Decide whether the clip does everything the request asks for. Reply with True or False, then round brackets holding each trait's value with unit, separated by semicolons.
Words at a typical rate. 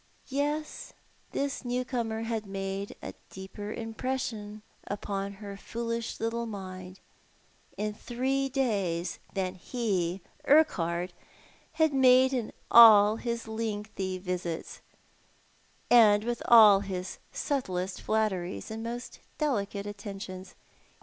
False (105 wpm)